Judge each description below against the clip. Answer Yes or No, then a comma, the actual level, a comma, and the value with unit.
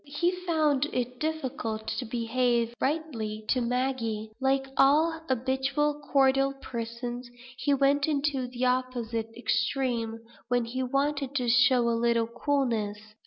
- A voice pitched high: Yes, very high, 255 Hz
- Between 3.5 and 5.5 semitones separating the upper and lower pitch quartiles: No, average, 2.9 semitones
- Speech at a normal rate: No, slow, 125 wpm